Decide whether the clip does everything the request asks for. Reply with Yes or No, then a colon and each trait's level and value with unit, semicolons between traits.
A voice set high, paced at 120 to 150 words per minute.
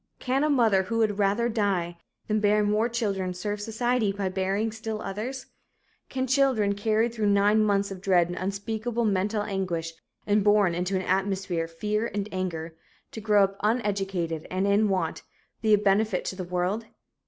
No: high, 205 Hz; average, 175 wpm